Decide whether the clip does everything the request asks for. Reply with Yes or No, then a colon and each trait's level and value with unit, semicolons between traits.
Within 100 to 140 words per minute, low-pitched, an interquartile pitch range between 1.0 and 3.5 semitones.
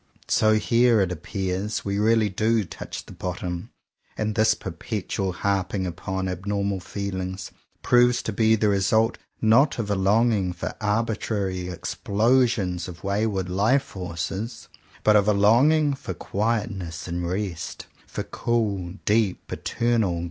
Yes: slow, 135 wpm; low, 100 Hz; average, 3.2 semitones